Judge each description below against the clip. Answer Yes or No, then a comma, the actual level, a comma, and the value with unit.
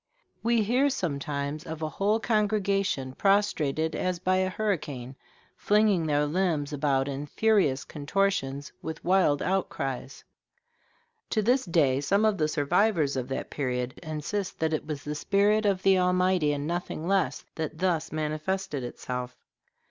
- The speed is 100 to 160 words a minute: Yes, average, 145 wpm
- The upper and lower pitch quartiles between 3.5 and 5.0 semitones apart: No, wide, 5.4 semitones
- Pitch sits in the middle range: Yes, medium, 160 Hz